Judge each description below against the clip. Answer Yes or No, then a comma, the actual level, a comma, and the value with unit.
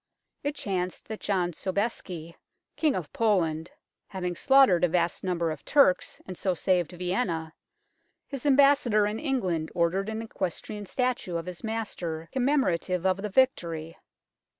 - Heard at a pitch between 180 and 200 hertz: Yes, medium, 185 Hz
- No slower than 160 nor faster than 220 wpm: No, average, 145 wpm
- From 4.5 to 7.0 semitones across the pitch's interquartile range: Yes, average, 4.8 semitones